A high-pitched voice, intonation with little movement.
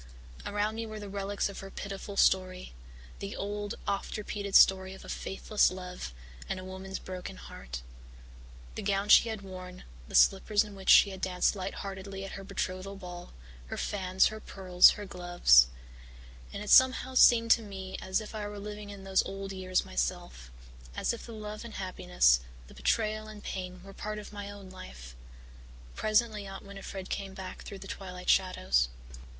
Yes: high, 195 Hz; narrow, 2.0 semitones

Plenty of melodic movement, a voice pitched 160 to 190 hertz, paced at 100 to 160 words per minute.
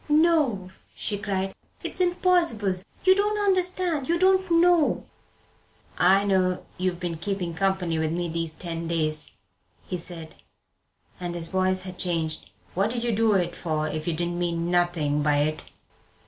Yes: wide, 6.6 semitones; medium, 185 Hz; average, 155 wpm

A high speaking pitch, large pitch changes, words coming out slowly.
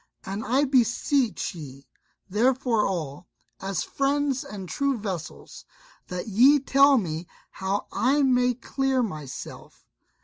Yes: high, 230 Hz; wide, 6.4 semitones; slow, 115 wpm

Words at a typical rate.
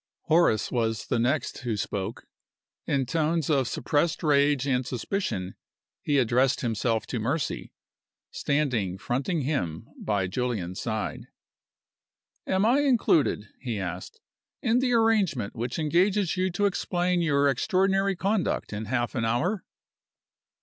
No: slow, 130 wpm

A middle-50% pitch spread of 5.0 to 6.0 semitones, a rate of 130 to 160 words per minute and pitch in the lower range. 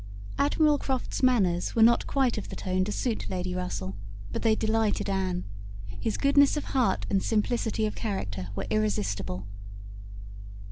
No: wide, 5.4 semitones; average, 150 wpm; high, 210 Hz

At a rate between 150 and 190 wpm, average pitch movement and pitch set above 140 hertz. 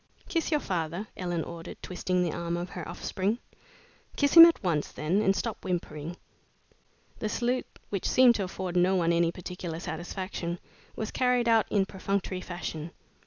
Yes: average, 165 wpm; average, 3.6 semitones; medium, 185 Hz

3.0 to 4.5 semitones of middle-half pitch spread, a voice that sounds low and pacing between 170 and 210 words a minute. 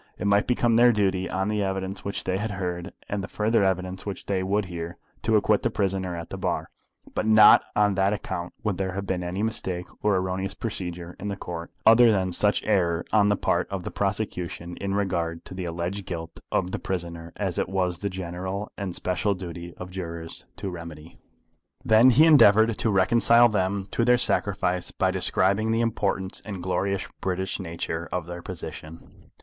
No: narrow, 2.5 semitones; very low, 95 Hz; average, 195 wpm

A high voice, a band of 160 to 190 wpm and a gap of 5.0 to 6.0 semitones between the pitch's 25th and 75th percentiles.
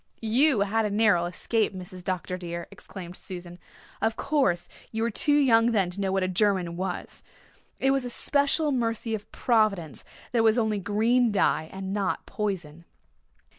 No: high, 205 Hz; average, 170 wpm; average, 3.9 semitones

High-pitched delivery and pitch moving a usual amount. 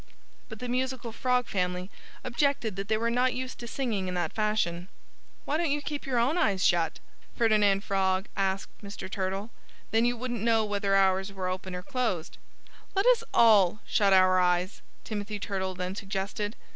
Yes: high, 205 Hz; average, 4.2 semitones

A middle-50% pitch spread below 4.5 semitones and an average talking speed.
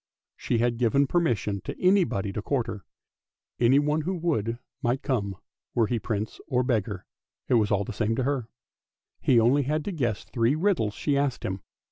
No: average, 4.8 semitones; average, 185 wpm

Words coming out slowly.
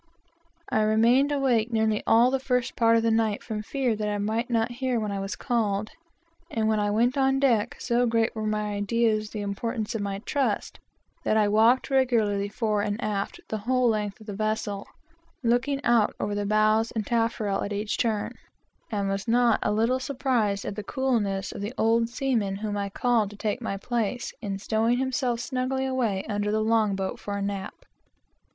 No: average, 200 wpm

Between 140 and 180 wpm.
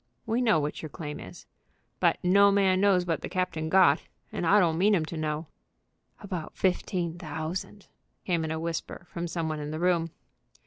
No: average, 190 wpm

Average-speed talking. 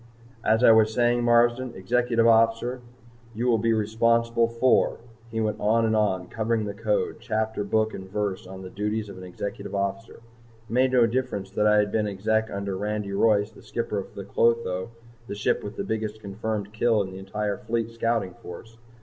Yes: average, 195 wpm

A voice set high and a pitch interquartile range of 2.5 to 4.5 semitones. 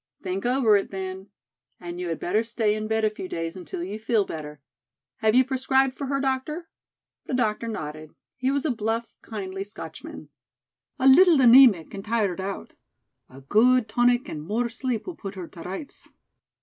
No: high, 220 Hz; average, 5.2 semitones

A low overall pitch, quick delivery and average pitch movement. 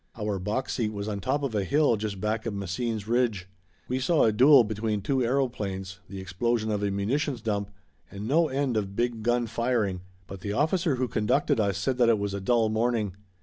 Yes: low, 110 Hz; fast, 210 wpm; average, 3.6 semitones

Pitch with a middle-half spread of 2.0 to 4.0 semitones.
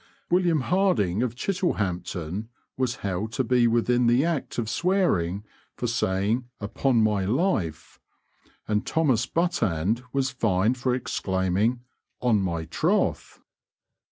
No: average, 5.1 semitones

